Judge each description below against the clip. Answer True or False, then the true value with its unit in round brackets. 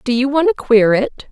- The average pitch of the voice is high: True (255 Hz)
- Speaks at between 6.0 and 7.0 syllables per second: False (5.4 syllables/s)